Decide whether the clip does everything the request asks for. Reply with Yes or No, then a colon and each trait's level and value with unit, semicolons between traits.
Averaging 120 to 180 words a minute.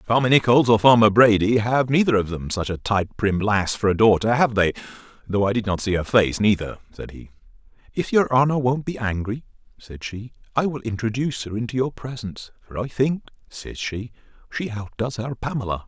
No: average, 195 wpm